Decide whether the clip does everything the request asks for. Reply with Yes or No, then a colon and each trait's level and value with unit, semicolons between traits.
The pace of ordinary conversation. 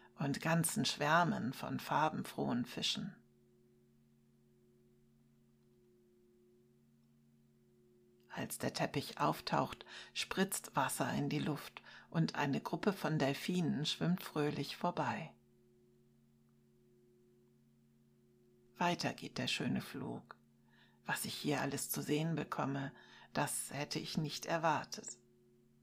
No: slow, 95 wpm